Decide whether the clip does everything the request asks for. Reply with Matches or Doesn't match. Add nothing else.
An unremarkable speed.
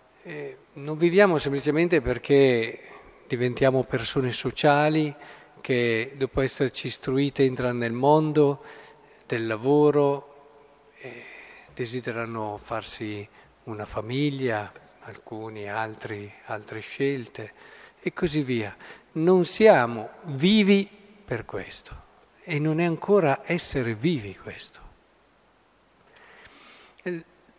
Doesn't match